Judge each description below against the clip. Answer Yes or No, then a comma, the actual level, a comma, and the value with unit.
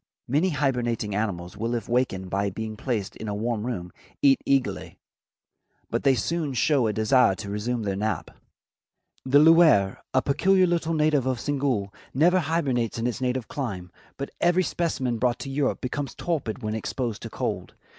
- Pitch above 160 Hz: No, low, 125 Hz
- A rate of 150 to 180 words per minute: Yes, average, 170 wpm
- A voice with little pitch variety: No, average, 4.9 semitones